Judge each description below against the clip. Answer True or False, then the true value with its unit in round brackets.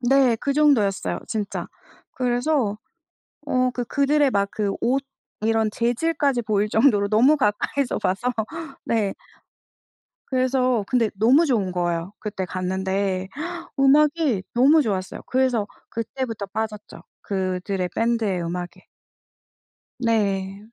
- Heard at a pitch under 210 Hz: False (225 Hz)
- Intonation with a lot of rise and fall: False (4.6 semitones)